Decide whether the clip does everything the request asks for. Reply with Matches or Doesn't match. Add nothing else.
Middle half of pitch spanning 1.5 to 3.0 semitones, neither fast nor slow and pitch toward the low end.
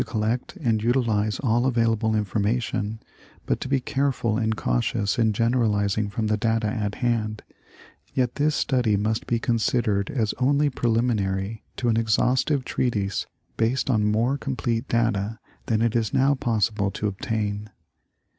Matches